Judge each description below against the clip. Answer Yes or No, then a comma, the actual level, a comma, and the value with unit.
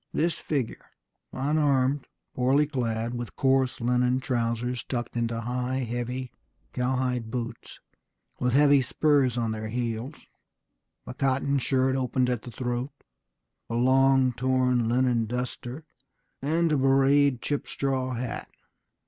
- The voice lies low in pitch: Yes, low, 125 Hz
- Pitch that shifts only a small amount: Yes, narrow, 1.8 semitones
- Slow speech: Yes, slow, 125 wpm